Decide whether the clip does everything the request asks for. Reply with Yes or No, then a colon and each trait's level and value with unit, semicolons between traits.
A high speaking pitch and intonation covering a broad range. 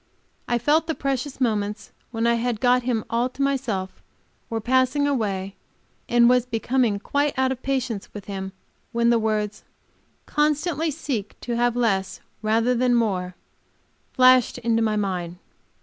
No: high, 235 Hz; average, 3.4 semitones